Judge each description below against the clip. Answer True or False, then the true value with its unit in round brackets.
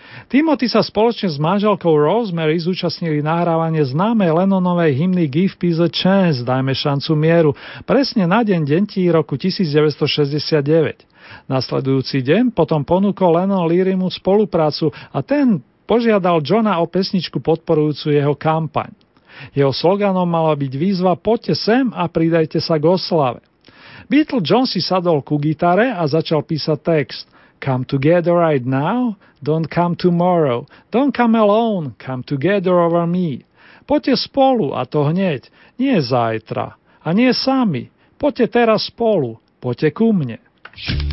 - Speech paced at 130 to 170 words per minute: True (135 wpm)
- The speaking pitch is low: False (170 Hz)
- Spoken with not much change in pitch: False (4.8 semitones)